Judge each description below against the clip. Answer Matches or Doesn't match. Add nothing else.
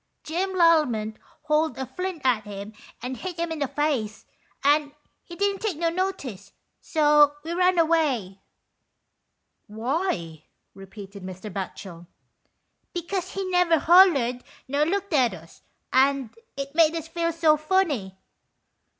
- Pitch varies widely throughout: Matches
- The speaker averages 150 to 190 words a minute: Doesn't match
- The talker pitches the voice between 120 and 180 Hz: Doesn't match